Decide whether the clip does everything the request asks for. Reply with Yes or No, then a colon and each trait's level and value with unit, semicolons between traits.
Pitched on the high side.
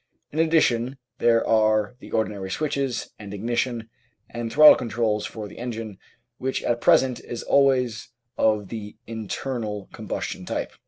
No: low, 115 Hz